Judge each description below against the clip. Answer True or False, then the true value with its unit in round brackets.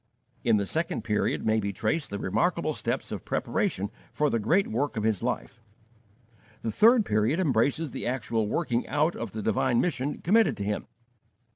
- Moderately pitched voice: False (115 Hz)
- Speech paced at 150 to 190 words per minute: True (175 wpm)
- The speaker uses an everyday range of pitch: False (6.5 semitones)